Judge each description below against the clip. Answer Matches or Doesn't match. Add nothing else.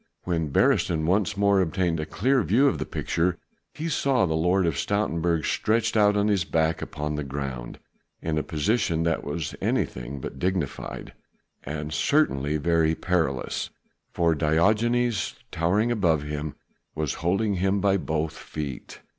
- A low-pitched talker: Matches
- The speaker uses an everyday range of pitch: Matches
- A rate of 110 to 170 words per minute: Matches